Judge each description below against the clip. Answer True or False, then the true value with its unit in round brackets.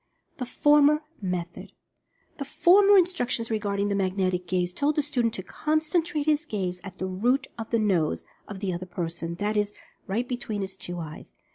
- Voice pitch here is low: False (210 Hz)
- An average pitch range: False (7.5 semitones)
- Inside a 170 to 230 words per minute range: True (175 wpm)